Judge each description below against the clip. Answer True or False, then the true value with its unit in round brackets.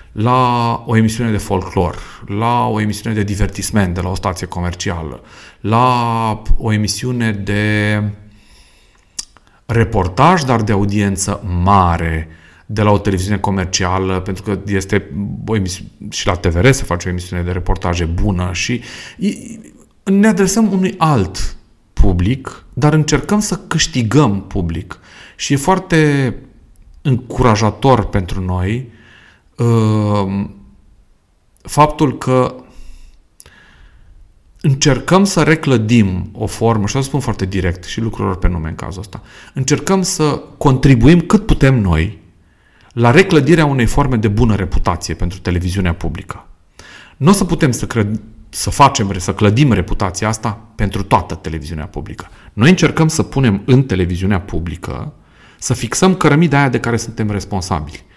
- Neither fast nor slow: True (130 wpm)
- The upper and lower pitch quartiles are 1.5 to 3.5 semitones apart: False (5.3 semitones)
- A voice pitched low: True (105 Hz)